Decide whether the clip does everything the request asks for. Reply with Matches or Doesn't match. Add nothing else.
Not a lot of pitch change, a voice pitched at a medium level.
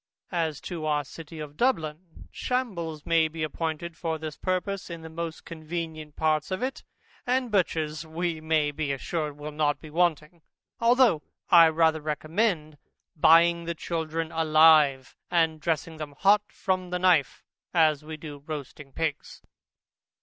Matches